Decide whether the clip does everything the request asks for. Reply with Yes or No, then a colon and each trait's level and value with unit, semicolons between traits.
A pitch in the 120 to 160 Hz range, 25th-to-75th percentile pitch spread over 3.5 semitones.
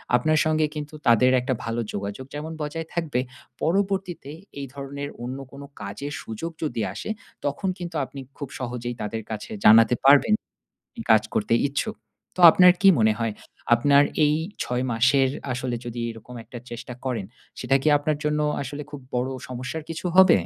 Yes: low, 135 Hz; average, 4.3 semitones